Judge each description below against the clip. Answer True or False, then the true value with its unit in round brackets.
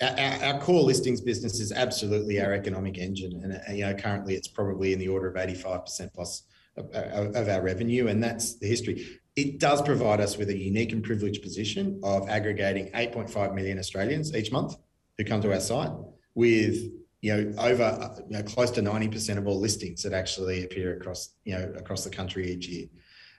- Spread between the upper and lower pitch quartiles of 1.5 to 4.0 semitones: True (3.3 semitones)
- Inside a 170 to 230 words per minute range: True (200 wpm)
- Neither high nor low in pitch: False (100 Hz)